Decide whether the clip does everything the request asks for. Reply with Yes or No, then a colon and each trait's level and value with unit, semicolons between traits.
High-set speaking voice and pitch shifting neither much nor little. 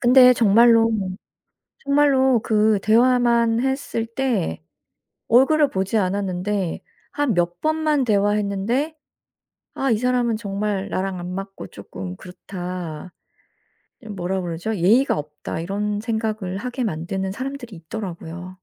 Yes: high, 210 Hz; average, 4.9 semitones